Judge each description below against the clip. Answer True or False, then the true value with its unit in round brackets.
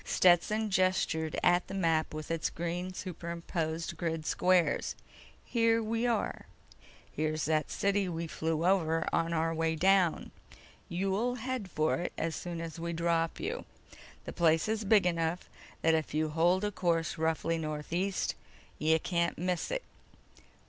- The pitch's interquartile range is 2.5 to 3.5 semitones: True (2.8 semitones)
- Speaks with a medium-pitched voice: True (170 Hz)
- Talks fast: False (150 wpm)